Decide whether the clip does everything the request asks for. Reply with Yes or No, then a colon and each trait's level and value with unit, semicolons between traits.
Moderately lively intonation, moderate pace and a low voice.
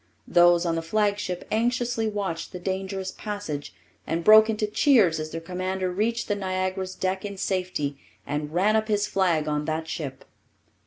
No: average, 4.0 semitones; average, 165 wpm; medium, 185 Hz